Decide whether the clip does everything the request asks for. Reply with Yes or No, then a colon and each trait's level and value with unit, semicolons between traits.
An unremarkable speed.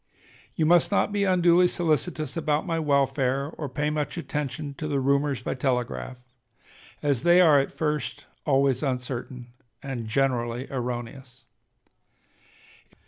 No: slow, 130 wpm